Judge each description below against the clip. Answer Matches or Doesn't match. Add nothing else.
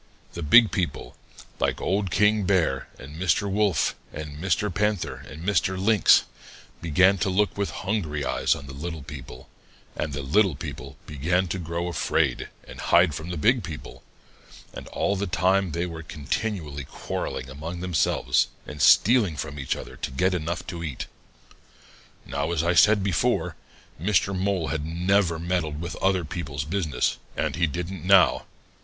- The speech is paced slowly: Doesn't match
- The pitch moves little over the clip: Doesn't match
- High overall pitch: Doesn't match